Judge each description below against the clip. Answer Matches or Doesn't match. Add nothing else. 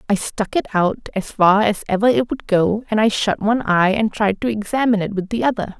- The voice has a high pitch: Matches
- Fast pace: Matches